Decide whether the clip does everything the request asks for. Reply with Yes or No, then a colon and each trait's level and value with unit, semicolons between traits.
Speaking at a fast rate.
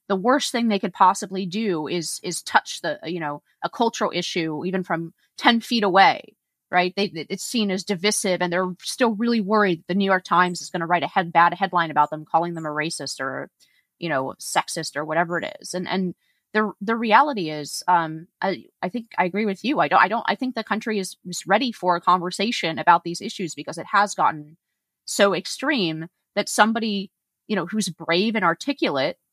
Yes: fast, 210 wpm